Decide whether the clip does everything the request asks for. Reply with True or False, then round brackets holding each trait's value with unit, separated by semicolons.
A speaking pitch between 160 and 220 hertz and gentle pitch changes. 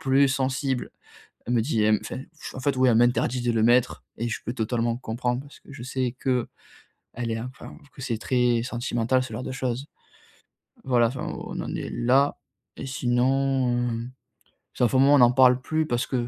False (125 Hz; 1.8 semitones)